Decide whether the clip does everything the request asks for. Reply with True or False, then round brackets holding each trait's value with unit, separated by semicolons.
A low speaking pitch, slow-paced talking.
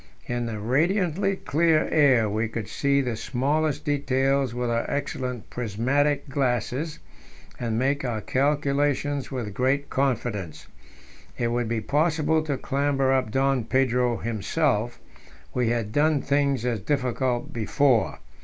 True (130 Hz; 130 wpm)